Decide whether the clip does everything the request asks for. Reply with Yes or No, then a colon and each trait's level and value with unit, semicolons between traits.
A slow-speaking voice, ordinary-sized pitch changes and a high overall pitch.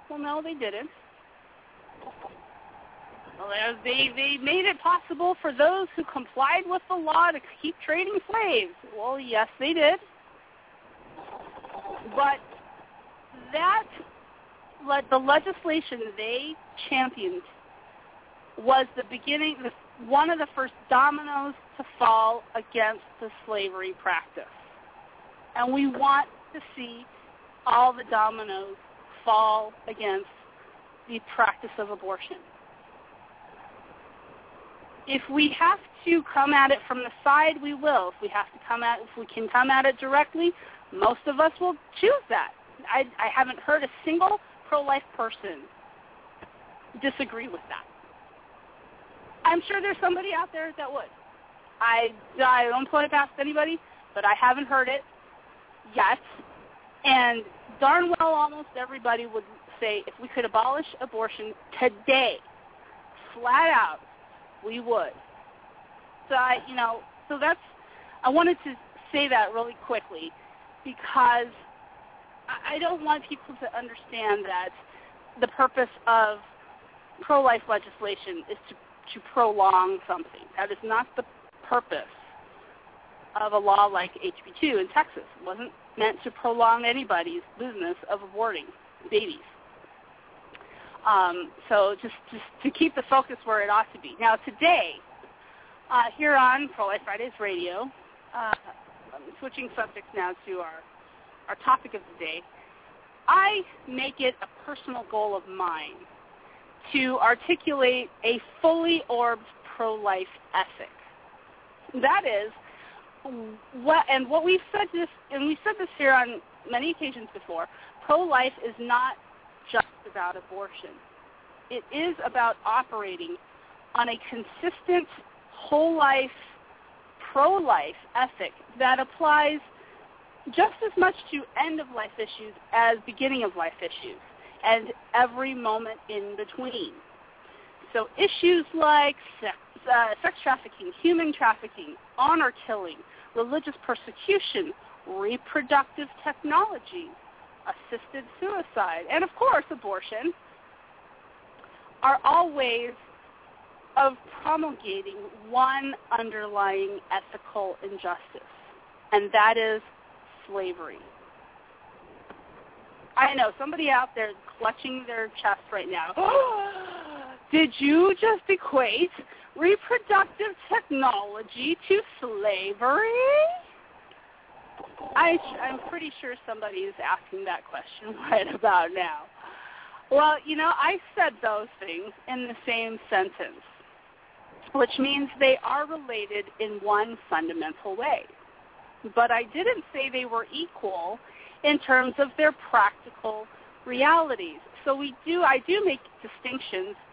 No: slow, 120 wpm; wide, 6.3 semitones; very high, 270 Hz